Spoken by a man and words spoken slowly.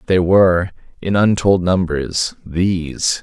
Yes: male; slow, 95 wpm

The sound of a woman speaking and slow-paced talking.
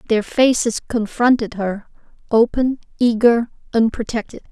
Yes: female; slow, 95 wpm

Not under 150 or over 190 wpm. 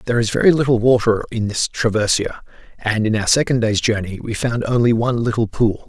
No: fast, 205 wpm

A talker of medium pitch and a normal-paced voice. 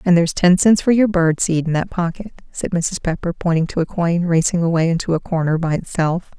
No: medium, 170 Hz; fast, 235 wpm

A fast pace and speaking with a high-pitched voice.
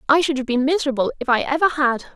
Yes: fast, 250 wpm; very high, 285 Hz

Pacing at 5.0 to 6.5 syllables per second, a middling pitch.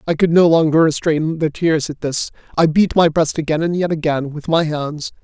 Yes: 5.1 syllables/s; medium, 160 Hz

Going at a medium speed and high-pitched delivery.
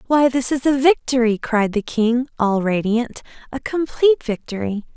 Yes: average, 155 wpm; high, 245 Hz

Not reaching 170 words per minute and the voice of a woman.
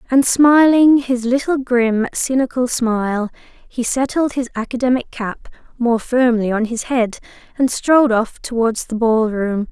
Yes: average, 140 wpm; female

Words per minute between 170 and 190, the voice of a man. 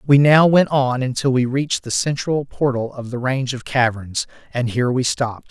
No: fast, 205 wpm; male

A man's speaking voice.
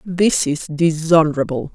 No: female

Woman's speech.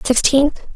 Yes: female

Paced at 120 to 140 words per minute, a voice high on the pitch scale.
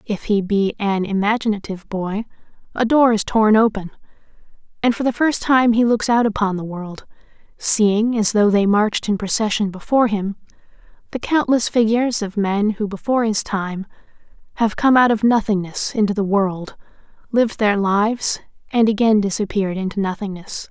No: average, 160 wpm; high, 210 Hz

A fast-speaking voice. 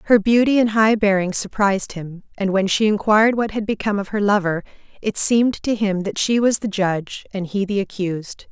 Yes: fast, 210 wpm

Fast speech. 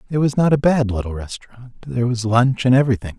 Yes: fast, 225 wpm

